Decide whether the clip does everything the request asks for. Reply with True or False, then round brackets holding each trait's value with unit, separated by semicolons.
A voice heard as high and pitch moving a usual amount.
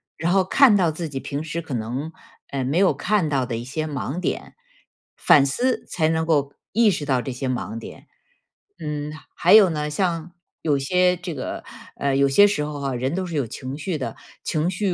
False (150 Hz; 4.4 semitones)